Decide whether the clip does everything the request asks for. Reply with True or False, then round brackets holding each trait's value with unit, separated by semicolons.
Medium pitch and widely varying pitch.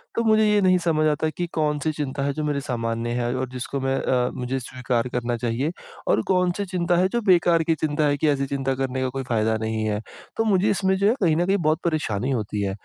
True (145 Hz; 5.7 semitones)